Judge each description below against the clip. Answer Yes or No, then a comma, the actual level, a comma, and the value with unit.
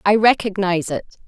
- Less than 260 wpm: Yes, average, 140 wpm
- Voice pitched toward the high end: Yes, high, 195 Hz